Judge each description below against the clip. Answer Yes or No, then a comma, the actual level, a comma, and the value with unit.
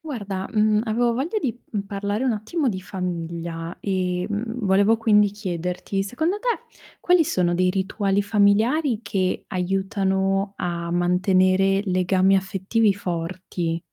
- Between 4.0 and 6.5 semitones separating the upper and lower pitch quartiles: No, average, 2.8 semitones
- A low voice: No, high, 195 Hz